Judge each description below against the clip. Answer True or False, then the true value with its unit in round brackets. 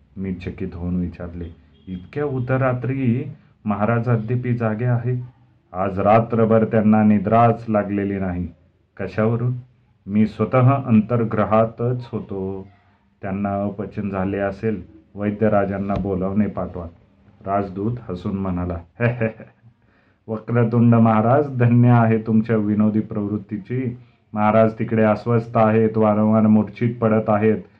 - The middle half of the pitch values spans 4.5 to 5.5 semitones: False (2.8 semitones)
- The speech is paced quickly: False (100 wpm)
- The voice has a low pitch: True (110 Hz)